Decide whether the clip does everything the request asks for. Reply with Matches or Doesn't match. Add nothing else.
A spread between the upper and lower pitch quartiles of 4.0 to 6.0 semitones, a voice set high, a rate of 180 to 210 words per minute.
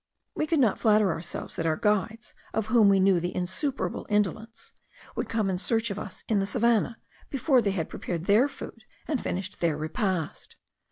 Doesn't match